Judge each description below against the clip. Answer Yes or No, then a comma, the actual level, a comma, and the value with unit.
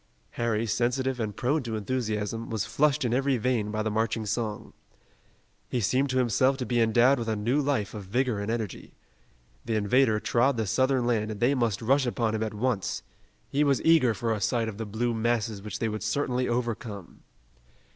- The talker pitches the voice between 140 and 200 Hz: No, low, 115 Hz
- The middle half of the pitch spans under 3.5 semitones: Yes, average, 2.9 semitones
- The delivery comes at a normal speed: Yes, average, 195 wpm